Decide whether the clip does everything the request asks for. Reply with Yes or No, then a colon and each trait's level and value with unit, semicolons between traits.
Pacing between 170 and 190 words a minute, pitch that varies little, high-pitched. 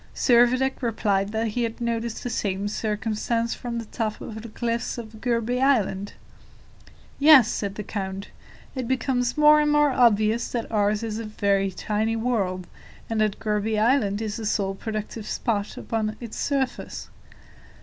No: average, 160 wpm; narrow, 2.3 semitones; high, 225 Hz